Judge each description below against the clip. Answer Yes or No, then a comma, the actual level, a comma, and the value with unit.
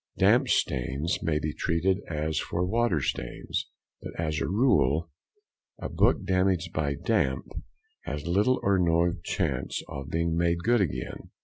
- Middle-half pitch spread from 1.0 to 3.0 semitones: No, average, 3.5 semitones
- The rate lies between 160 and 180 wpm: No, average, 145 wpm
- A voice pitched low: Yes, very low, 85 Hz